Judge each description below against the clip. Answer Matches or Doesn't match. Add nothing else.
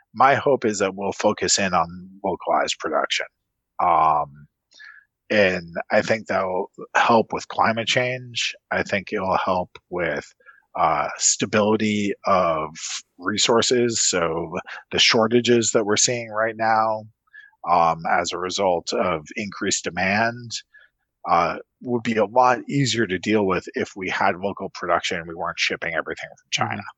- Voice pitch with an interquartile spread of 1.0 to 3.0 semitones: Matches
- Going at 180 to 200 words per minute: Doesn't match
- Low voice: Matches